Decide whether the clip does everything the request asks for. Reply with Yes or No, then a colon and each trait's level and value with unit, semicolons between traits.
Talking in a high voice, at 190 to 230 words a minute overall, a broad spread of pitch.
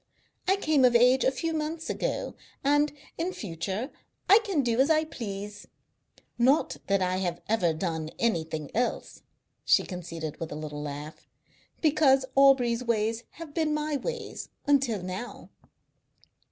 No: high, 240 Hz; average, 140 wpm; wide, 8.4 semitones